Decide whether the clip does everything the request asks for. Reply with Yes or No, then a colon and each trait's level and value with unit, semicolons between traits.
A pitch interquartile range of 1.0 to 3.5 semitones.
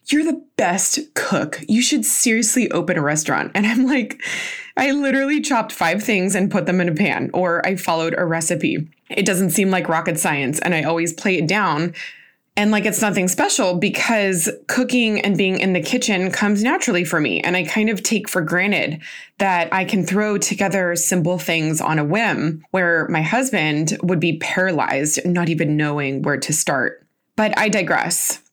No: average, 4.3 semitones